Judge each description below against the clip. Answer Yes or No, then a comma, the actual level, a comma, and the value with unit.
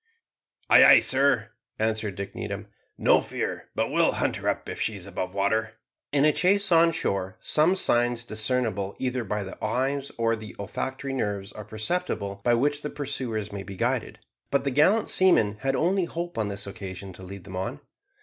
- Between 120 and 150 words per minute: No, average, 190 wpm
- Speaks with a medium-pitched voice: No, low, 115 Hz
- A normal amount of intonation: No, wide, 5.7 semitones